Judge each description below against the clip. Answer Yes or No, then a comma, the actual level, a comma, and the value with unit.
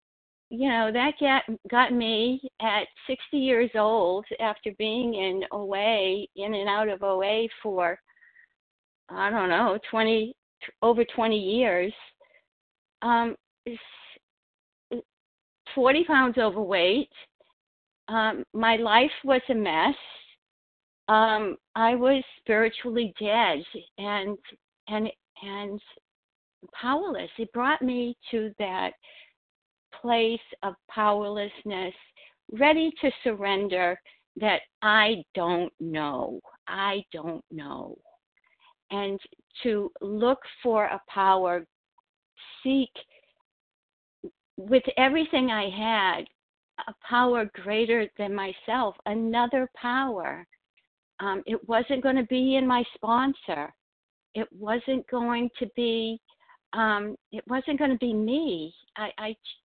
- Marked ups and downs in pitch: No, average, 3.8 semitones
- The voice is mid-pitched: No, high, 225 Hz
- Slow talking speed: Yes, slow, 105 wpm